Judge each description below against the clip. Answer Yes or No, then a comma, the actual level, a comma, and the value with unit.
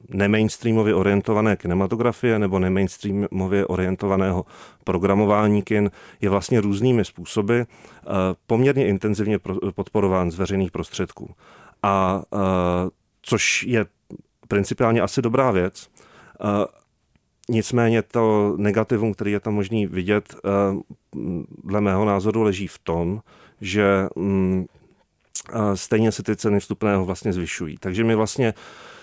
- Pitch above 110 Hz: No, low, 100 Hz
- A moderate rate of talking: No, slow, 105 wpm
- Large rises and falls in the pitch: No, narrow, 2.4 semitones